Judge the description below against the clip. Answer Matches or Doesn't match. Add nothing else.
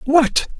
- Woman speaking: Doesn't match